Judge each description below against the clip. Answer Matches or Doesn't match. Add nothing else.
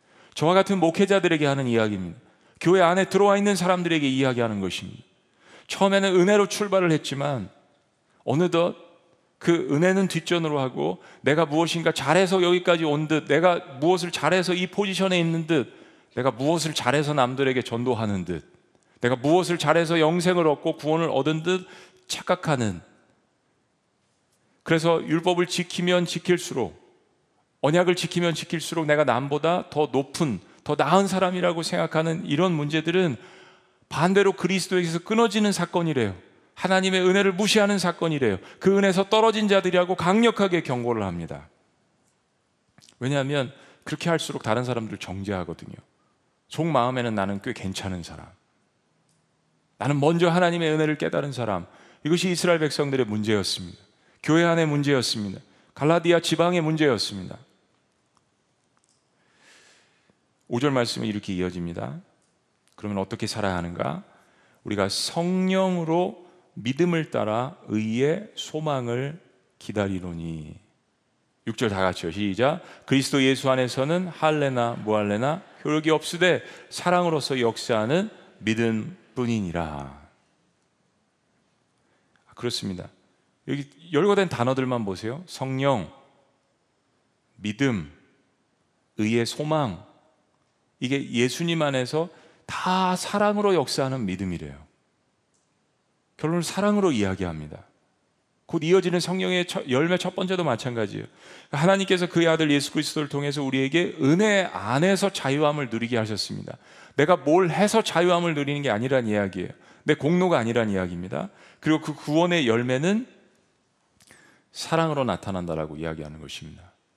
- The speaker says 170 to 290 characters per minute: Doesn't match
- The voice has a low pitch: Doesn't match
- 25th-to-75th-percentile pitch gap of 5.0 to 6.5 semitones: Doesn't match